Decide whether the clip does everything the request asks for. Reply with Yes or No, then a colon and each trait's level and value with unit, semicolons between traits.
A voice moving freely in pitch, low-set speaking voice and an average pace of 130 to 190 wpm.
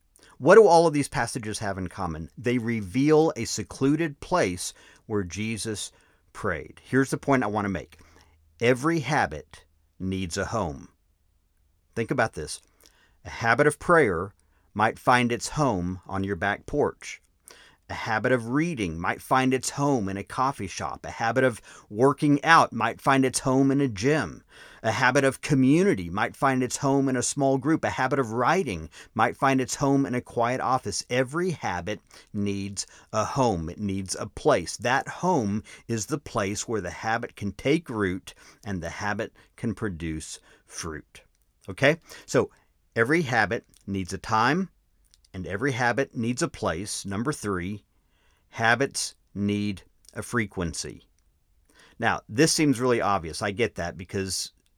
Yes: wide, 6.0 semitones; low, 110 Hz; average, 160 wpm